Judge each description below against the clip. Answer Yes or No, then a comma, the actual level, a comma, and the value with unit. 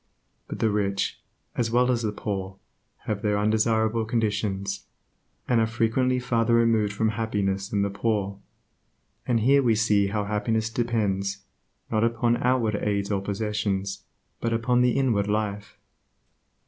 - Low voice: Yes, low, 110 Hz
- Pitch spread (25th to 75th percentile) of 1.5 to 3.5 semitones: Yes, narrow, 2.4 semitones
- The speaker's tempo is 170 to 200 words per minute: No, average, 145 wpm